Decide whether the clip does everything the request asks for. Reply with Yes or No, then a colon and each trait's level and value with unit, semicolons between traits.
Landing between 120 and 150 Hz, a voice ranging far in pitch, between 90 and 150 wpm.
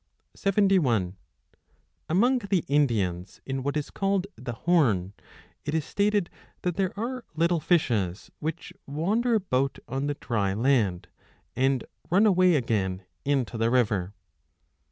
Yes: medium, 140 Hz; wide, 8.0 semitones; slow, 135 wpm